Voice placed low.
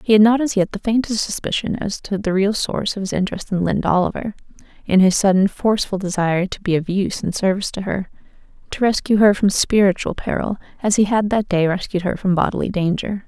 No: high, 200 Hz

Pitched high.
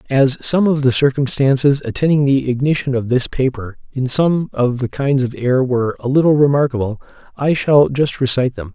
No: low, 135 Hz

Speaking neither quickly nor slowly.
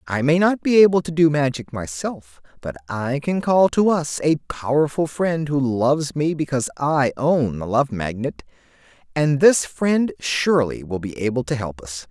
Yes: average, 185 wpm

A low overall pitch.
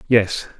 Yes: low, 105 Hz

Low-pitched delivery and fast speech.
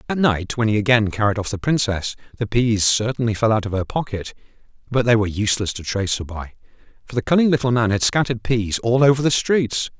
Yes: low, 115 Hz; fast, 220 wpm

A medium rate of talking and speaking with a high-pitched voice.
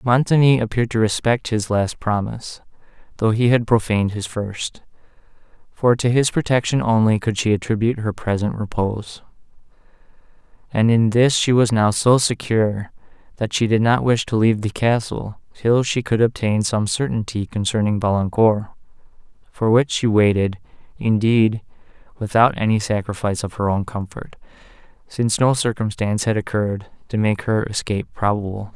No: average, 150 wpm; low, 110 Hz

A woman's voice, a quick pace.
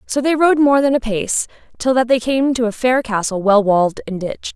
Yes: female; fast, 250 wpm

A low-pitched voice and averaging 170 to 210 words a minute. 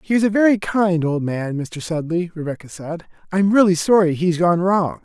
No: medium, 175 Hz; average, 200 wpm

